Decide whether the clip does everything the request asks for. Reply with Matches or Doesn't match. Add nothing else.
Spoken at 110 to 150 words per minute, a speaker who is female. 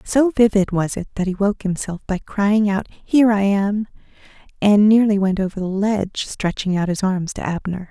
Doesn't match